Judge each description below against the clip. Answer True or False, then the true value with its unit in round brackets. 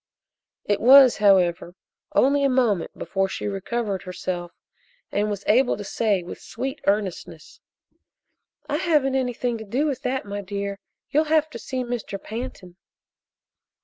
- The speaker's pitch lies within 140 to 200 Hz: False (215 Hz)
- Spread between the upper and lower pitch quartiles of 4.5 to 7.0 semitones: True (5.0 semitones)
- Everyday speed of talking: True (145 wpm)